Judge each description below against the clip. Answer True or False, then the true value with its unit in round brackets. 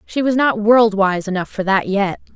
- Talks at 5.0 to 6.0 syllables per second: False (4.7 syllables/s)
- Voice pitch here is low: False (210 Hz)